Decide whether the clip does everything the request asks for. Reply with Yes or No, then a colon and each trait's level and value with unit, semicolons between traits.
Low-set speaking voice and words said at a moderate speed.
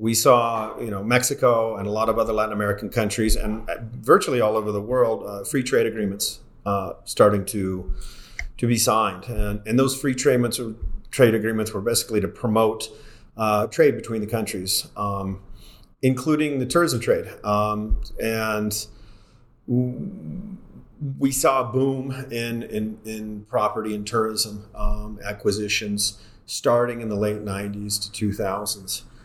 Yes: low, 110 Hz; average, 150 wpm